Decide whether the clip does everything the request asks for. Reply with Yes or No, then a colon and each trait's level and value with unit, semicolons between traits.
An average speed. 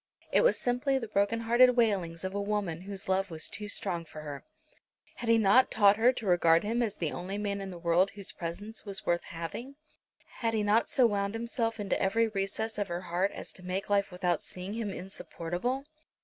No: fast, 210 wpm